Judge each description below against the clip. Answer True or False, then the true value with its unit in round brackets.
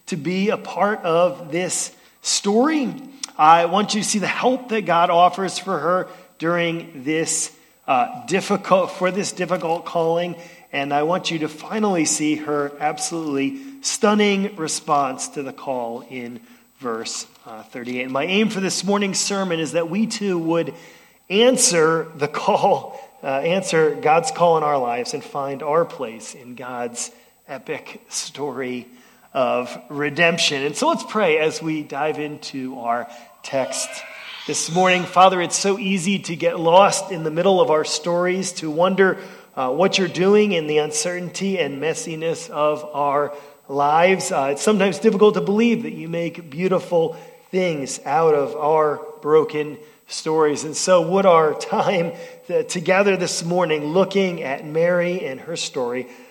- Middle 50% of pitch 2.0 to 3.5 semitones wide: False (4.1 semitones)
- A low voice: False (170 Hz)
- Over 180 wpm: False (155 wpm)